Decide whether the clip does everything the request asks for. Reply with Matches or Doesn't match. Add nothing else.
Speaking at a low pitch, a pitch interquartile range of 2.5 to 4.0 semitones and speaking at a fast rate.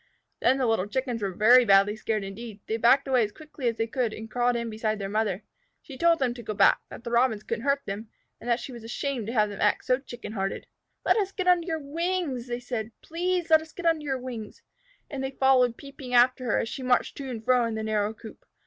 Doesn't match